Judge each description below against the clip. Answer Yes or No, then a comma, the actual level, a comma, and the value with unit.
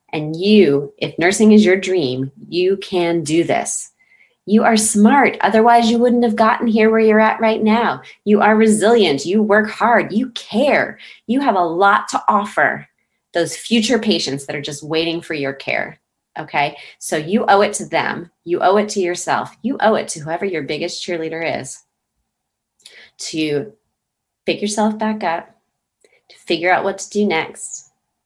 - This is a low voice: No, high, 200 Hz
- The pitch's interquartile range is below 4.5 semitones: No, average, 4.9 semitones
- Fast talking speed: No, average, 175 wpm